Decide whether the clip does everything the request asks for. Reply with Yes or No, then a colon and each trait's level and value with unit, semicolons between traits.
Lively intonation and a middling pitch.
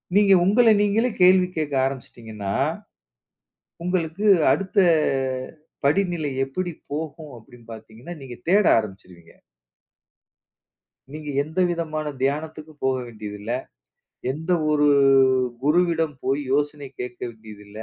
Yes: wide, 6.3 semitones; medium, 150 Hz